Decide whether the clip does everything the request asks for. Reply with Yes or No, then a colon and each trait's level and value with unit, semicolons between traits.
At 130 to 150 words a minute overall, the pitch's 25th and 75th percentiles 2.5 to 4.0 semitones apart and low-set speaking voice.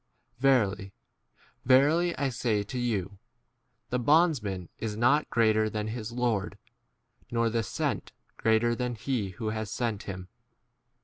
Yes: average, 140 wpm; average, 2.9 semitones; low, 115 Hz